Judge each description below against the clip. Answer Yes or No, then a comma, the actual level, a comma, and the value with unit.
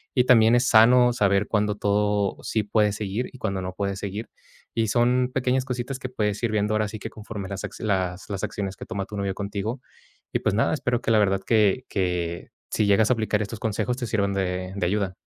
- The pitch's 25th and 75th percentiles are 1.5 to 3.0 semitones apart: Yes, average, 2.7 semitones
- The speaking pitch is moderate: No, low, 105 Hz